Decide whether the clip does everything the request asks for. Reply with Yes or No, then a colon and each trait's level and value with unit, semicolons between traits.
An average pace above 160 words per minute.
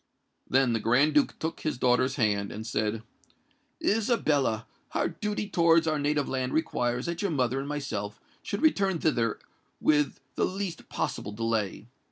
No: average, 155 wpm